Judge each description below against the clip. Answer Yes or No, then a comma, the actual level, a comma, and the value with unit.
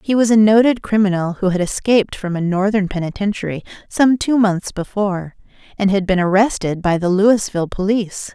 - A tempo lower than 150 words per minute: No, average, 170 wpm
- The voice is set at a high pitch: Yes, high, 200 Hz